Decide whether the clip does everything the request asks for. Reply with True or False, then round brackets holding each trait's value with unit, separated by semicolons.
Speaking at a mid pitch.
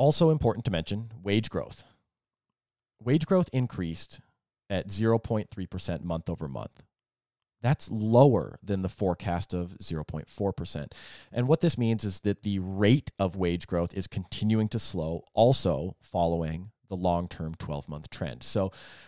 False (100 Hz)